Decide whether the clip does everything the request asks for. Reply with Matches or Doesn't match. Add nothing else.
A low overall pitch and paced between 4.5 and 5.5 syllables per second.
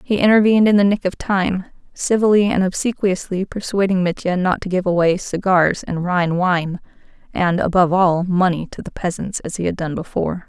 Doesn't match